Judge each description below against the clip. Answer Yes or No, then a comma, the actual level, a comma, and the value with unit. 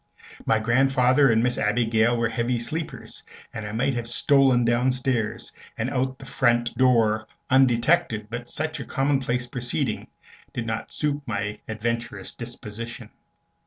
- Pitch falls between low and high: No, low, 120 Hz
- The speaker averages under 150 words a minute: Yes, average, 140 wpm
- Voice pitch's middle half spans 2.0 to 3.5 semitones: Yes, narrow, 2.6 semitones